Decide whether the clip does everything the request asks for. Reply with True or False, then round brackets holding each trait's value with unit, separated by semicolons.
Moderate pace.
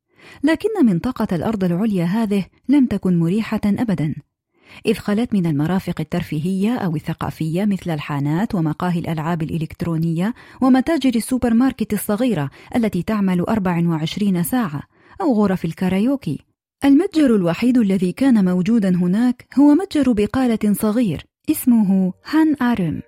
True (115 wpm)